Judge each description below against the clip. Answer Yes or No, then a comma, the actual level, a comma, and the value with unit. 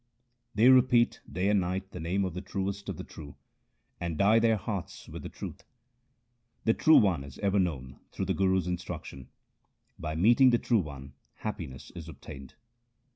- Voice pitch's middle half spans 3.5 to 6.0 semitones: Yes, average, 4.7 semitones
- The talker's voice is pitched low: Yes, very low, 95 Hz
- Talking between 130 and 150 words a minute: No, average, 180 wpm